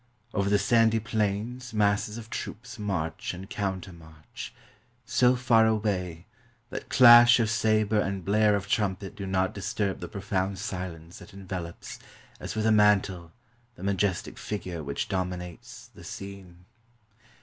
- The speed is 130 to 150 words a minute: Yes, average, 140 wpm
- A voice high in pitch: No, low, 100 Hz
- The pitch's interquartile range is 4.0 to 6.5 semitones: No, average, 2.7 semitones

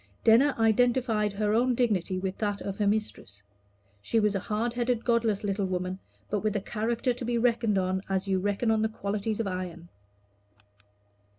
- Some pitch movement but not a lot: Yes, average, 3.1 semitones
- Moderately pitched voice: No, high, 210 Hz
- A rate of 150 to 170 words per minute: No, average, 180 wpm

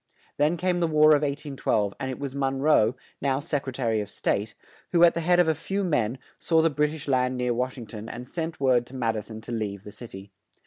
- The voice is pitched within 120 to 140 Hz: Yes, low, 135 Hz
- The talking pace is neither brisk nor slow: No, fast, 265 wpm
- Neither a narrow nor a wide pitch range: Yes, average, 4.9 semitones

